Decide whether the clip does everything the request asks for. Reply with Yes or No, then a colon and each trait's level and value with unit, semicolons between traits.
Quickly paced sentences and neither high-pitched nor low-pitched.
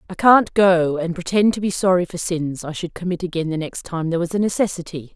Yes: fast, 245 wpm; medium, 175 Hz